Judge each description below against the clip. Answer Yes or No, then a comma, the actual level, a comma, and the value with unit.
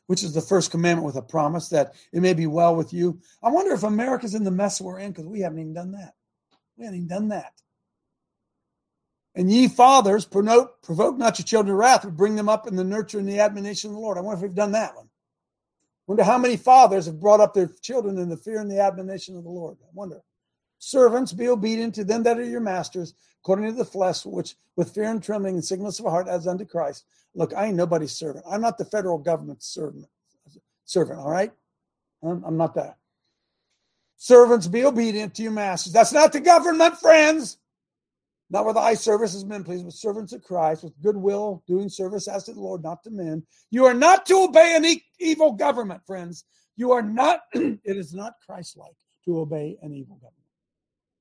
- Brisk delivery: Yes, fast, 215 wpm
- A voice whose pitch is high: Yes, high, 200 Hz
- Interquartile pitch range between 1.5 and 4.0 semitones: No, average, 4.4 semitones